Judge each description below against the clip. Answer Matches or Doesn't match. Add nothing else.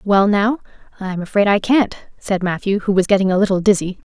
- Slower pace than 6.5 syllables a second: Matches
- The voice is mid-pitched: Doesn't match